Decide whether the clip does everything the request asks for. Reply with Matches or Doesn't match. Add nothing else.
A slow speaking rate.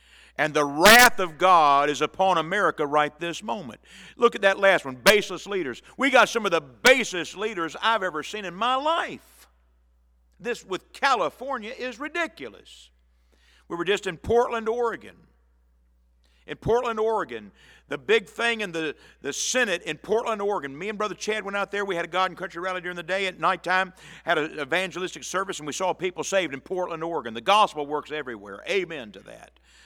Doesn't match